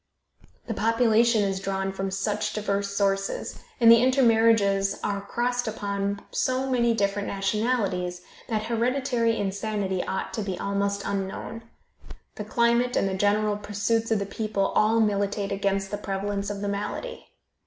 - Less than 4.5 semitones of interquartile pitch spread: Yes, narrow, 2.4 semitones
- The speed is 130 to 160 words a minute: Yes, average, 145 wpm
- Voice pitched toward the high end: Yes, high, 205 Hz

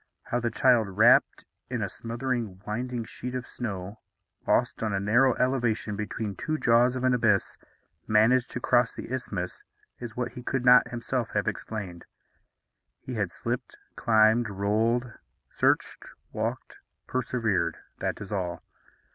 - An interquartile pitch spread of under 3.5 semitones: Yes, average, 2.9 semitones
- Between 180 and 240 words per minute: No, average, 145 wpm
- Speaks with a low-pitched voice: Yes, low, 115 Hz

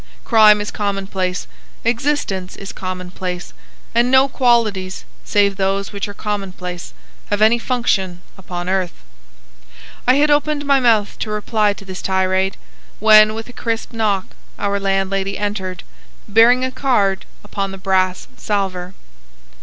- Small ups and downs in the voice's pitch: No, average, 3.2 semitones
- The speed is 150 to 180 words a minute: No, slow, 135 wpm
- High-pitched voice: Yes, high, 200 Hz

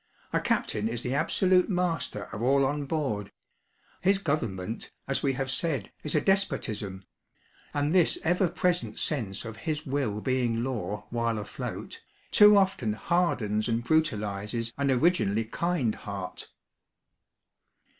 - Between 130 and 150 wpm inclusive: Yes, slow, 135 wpm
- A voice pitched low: Yes, low, 130 Hz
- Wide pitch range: Yes, wide, 7.1 semitones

